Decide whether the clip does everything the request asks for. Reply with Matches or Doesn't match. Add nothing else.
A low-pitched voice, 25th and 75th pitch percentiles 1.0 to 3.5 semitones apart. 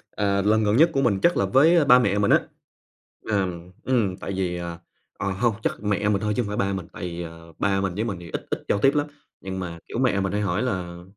Matches